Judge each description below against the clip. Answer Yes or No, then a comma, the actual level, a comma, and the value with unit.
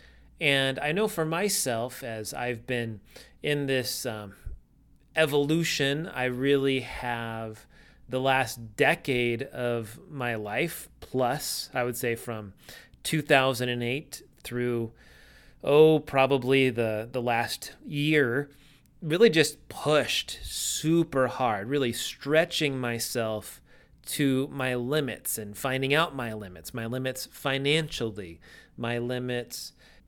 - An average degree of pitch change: Yes, average, 3.7 semitones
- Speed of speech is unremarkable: No, slow, 110 wpm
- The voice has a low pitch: Yes, low, 130 Hz